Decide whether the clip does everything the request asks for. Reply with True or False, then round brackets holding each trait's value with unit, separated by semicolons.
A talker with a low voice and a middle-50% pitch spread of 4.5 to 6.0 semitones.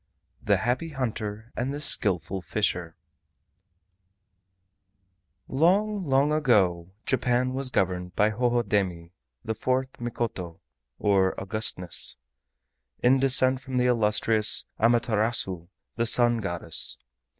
True (115 Hz; 5.0 semitones)